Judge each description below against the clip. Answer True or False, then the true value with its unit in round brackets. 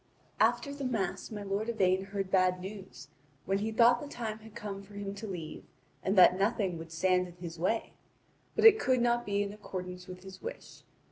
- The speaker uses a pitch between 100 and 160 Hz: False (200 Hz)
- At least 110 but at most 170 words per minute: False (205 wpm)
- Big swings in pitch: False (3.3 semitones)